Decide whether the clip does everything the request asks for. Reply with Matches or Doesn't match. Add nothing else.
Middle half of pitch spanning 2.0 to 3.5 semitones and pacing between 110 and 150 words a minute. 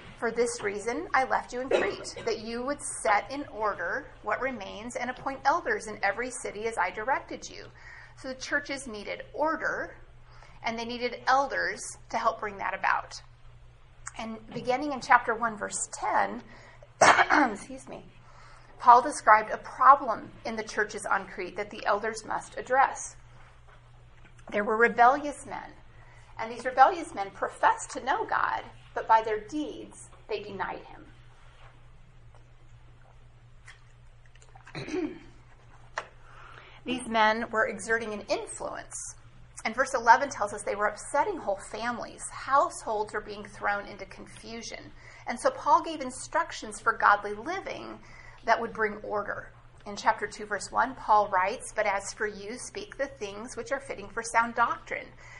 Doesn't match